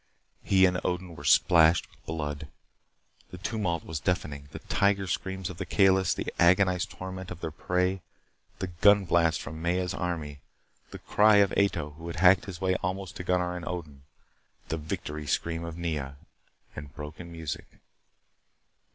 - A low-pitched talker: Yes, very low, 90 Hz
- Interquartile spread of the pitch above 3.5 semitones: No, average, 2.8 semitones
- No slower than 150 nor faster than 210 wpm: Yes, average, 160 wpm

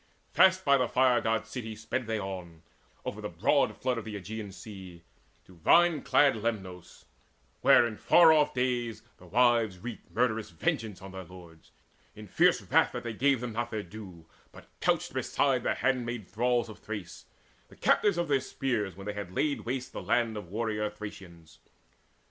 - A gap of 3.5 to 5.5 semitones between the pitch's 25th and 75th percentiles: Yes, average, 4.4 semitones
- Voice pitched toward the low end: Yes, low, 110 Hz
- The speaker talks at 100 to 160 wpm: No, average, 180 wpm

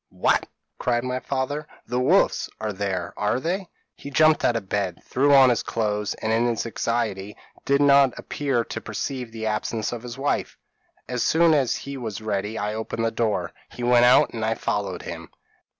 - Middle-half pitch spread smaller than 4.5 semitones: Yes, average, 4.0 semitones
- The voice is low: Yes, low, 115 Hz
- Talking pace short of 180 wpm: No, average, 195 wpm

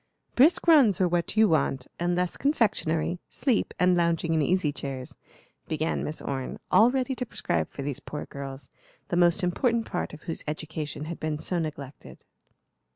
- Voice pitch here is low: No, medium, 170 Hz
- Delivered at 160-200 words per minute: Yes, average, 170 wpm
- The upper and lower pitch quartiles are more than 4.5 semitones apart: Yes, average, 5.0 semitones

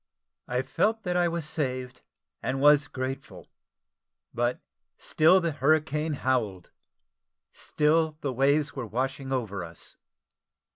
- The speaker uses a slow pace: Yes, slow, 115 wpm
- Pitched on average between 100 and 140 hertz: Yes, low, 135 Hz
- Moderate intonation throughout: Yes, average, 3.5 semitones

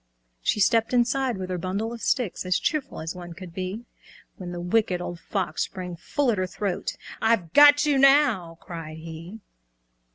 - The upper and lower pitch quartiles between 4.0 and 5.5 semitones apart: Yes, average, 5.2 semitones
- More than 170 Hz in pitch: Yes, high, 190 Hz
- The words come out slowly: No, average, 175 wpm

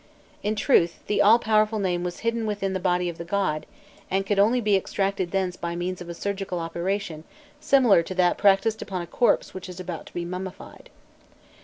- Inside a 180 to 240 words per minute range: Yes, average, 200 wpm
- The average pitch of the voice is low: No, high, 190 Hz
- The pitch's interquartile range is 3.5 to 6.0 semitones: No, average, 2.9 semitones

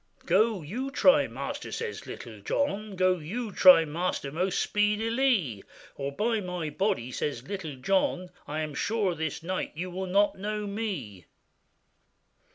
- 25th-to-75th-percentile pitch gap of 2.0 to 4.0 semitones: No, average, 5.3 semitones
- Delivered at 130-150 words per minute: Yes, average, 145 wpm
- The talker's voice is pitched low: No, medium, 185 Hz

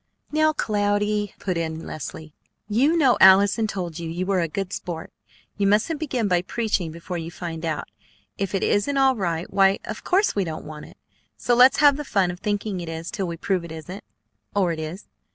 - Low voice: No, high, 195 Hz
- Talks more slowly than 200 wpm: No, fast, 205 wpm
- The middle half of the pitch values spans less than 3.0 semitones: No, average, 4.1 semitones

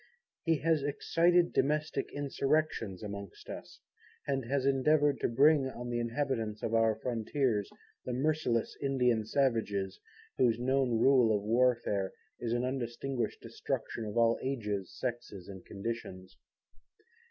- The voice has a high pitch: No, low, 120 Hz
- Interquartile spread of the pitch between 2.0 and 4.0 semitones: Yes, average, 3.7 semitones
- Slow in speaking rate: Yes, slow, 130 wpm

